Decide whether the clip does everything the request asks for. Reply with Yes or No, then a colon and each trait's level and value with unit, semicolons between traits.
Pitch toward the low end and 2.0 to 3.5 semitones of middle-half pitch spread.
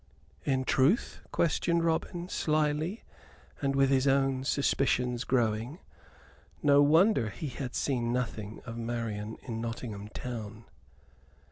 No: low, 130 Hz; average, 4.1 semitones